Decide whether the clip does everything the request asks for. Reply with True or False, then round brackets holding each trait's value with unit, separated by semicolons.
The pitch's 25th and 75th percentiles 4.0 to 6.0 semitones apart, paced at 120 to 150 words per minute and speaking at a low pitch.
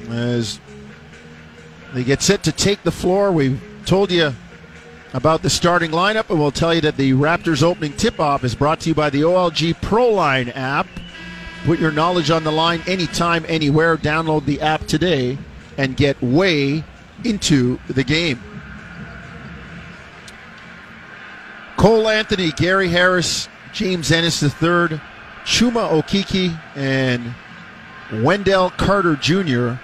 False (4.6 semitones; 135 wpm; 160 Hz)